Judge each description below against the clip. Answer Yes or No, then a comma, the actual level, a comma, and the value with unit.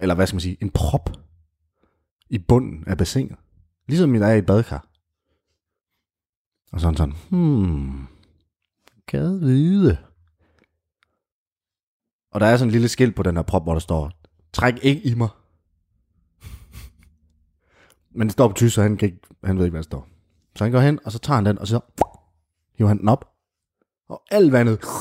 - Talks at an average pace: Yes, average, 175 wpm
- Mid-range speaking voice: No, very low, 95 Hz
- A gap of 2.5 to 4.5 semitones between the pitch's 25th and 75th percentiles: No, wide, 5.4 semitones